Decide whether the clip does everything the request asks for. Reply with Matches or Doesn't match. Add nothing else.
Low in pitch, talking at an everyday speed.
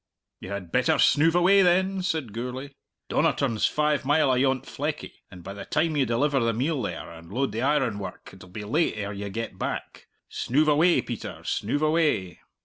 Matches